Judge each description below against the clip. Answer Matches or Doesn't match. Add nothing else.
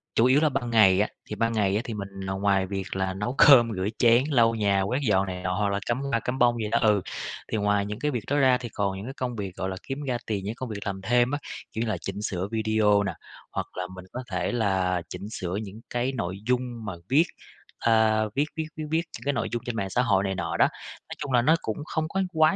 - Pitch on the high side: Doesn't match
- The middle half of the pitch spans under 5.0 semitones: Matches